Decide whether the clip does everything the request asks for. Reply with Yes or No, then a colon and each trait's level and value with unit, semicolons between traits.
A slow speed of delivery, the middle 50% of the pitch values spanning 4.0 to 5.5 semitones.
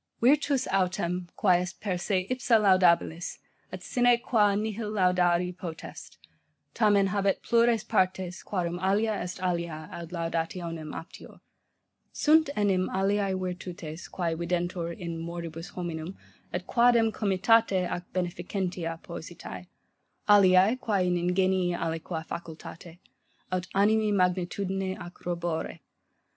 No: slow, 115 wpm; average, 2.8 semitones